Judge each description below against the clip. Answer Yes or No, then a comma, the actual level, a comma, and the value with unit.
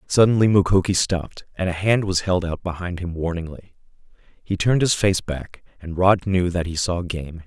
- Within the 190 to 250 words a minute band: Yes, average, 195 wpm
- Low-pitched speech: Yes, very low, 90 Hz